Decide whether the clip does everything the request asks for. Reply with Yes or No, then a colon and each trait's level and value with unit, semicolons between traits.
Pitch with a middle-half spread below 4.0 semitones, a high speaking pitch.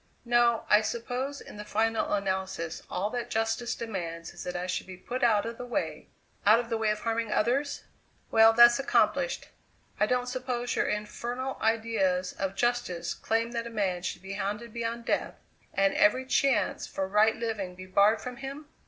Yes: average, 3.5 semitones; high, 225 Hz